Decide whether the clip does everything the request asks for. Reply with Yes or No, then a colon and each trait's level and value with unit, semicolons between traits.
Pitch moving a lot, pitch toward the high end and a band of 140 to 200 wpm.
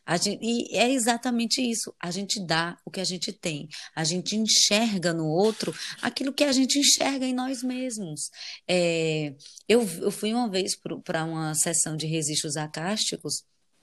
Yes: wide, 6.4 semitones; high, 195 Hz; average, 170 wpm